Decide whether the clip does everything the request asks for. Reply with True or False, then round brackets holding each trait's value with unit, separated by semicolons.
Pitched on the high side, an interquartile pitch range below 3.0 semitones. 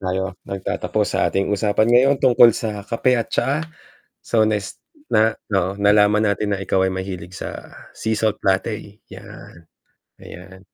False (105 Hz; 2.6 semitones)